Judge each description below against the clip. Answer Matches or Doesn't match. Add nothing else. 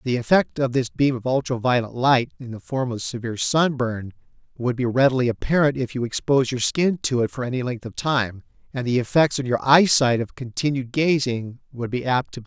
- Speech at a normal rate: Doesn't match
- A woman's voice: Doesn't match